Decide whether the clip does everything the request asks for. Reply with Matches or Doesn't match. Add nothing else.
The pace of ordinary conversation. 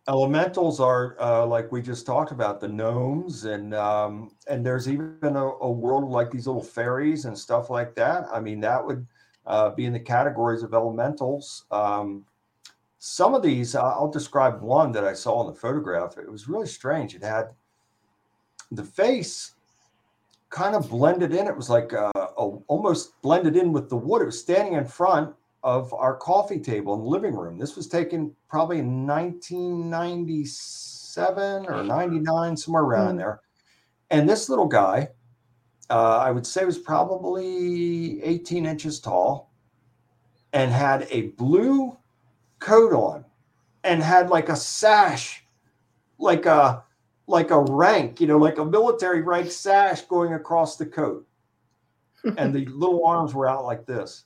Matches